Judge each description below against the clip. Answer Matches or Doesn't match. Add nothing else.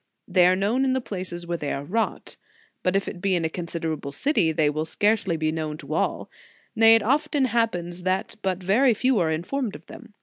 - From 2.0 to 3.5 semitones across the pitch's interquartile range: Doesn't match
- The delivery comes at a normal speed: Doesn't match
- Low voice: Doesn't match